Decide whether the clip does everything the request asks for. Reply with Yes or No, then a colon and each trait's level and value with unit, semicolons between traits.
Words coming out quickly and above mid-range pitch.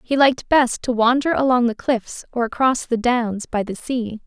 Yes: fast, 210 wpm; high, 240 Hz